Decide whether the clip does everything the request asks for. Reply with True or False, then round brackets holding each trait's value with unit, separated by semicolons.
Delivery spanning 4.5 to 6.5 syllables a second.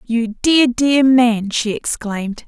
False (3.4 syllables/s)